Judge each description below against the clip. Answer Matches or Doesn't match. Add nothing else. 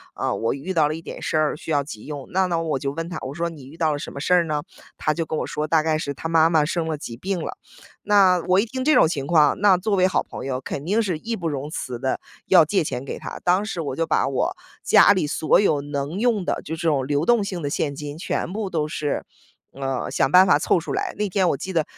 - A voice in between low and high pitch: Matches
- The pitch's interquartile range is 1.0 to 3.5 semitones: Doesn't match